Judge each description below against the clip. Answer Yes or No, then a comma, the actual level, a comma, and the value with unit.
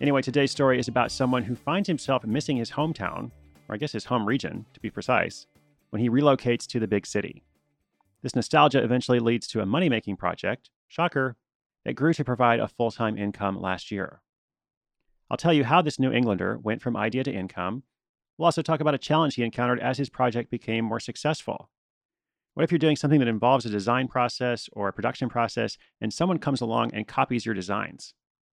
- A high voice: No, low, 120 Hz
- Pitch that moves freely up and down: No, average, 4.0 semitones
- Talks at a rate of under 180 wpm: No, average, 200 wpm